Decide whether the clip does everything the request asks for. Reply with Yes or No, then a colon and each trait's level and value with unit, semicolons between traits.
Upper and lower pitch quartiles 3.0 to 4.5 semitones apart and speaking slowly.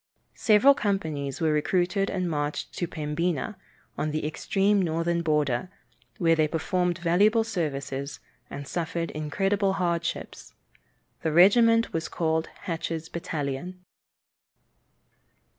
Yes: average, 3.6 semitones; slow, 110 wpm